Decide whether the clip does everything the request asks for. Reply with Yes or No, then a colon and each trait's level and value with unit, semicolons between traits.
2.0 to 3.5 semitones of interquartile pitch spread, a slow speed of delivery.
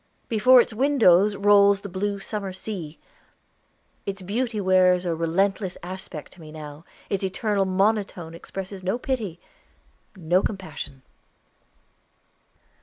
Yes: narrow, 2.5 semitones; slow, 115 wpm